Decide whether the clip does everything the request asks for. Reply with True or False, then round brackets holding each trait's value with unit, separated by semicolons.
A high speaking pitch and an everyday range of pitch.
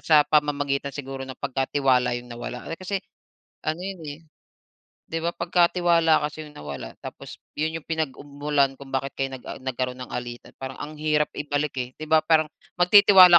False (145 Hz; 3.3 semitones)